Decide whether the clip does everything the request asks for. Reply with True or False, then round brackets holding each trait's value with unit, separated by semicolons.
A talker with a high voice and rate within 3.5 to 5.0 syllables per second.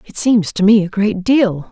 True (205 Hz; 4.5 syllables/s)